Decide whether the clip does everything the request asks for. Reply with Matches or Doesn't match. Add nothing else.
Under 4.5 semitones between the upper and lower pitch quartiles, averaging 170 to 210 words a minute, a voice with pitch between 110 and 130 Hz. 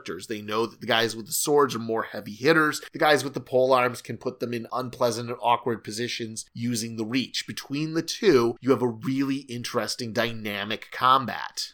Matches